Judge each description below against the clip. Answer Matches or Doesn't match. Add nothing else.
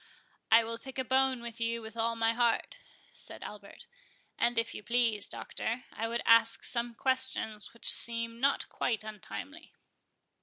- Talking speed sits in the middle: Matches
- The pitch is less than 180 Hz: Doesn't match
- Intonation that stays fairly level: Matches